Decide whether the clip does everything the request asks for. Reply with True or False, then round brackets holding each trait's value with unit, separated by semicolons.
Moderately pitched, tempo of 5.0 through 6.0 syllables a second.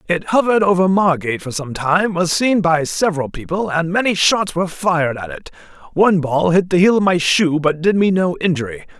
True (175 Hz; 5.6 syllables/s)